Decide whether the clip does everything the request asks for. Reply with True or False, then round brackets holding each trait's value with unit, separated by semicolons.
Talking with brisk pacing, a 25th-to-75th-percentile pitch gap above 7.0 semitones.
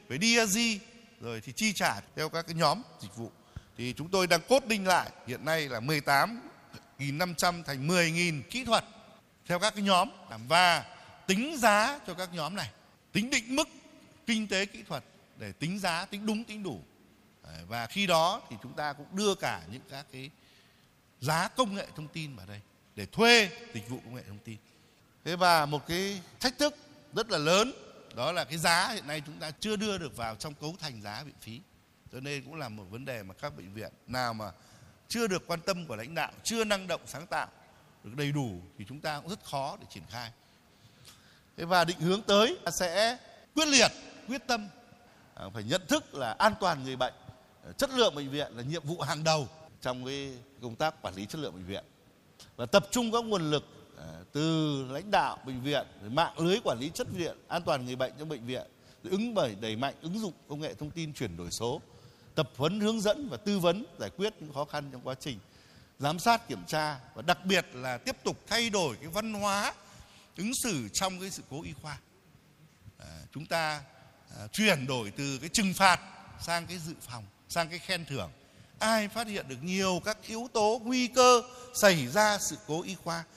False (210 wpm; 7.5 semitones)